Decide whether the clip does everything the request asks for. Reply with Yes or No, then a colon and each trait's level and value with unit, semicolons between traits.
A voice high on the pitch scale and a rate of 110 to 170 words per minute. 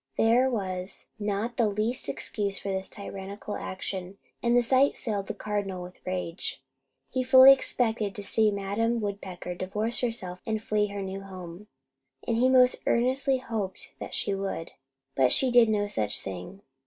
Yes: high, 205 Hz; average, 165 wpm